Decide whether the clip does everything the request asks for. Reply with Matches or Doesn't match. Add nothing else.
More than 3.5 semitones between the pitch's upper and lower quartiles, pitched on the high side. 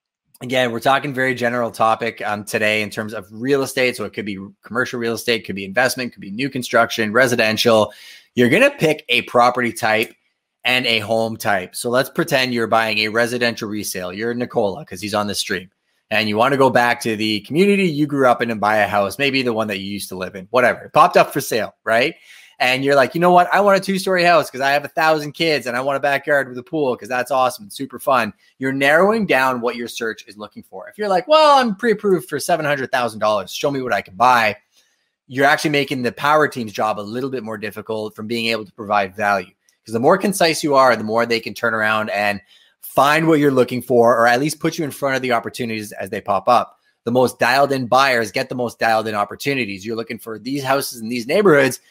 Doesn't match